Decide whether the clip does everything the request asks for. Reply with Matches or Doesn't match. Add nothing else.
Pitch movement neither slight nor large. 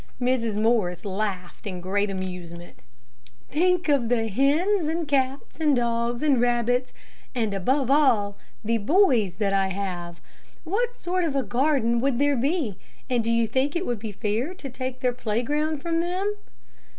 Doesn't match